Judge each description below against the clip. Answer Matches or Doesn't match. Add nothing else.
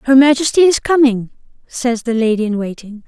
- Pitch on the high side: Matches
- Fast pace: Doesn't match